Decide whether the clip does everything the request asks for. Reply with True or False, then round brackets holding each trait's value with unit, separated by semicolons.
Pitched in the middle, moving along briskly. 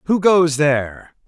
False (155 Hz; 140 wpm)